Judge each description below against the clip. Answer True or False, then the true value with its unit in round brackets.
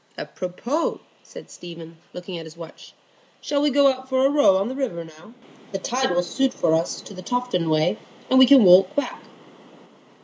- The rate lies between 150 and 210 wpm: True (195 wpm)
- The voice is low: False (195 Hz)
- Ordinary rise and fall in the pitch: False (7.3 semitones)